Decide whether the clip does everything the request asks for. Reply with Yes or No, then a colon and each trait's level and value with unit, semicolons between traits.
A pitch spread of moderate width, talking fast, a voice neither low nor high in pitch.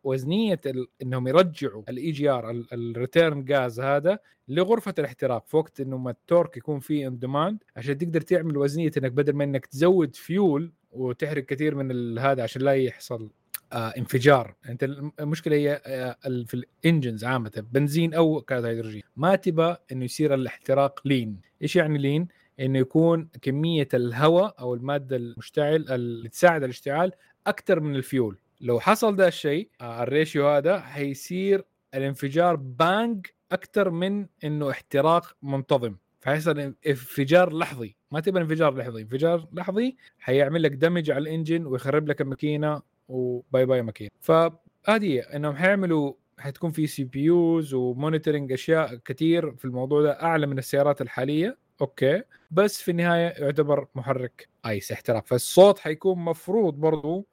Yes: average, 4.2 semitones; fast, 140 wpm; medium, 145 Hz